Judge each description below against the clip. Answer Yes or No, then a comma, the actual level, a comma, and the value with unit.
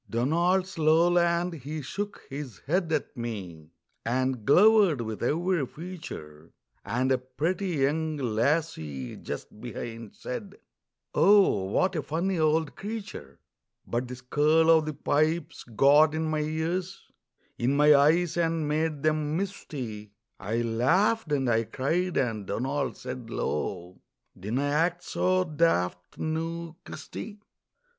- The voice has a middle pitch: Yes, medium, 150 Hz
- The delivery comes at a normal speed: No, slow, 125 wpm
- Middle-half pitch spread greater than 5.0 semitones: Yes, wide, 5.6 semitones